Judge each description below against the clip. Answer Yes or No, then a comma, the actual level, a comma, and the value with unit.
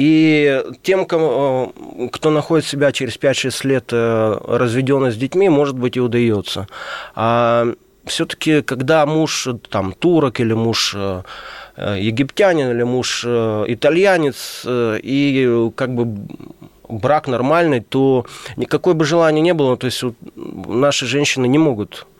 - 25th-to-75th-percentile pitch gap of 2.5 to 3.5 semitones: No, average, 4.0 semitones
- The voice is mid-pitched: No, low, 130 Hz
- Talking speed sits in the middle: Yes, average, 120 wpm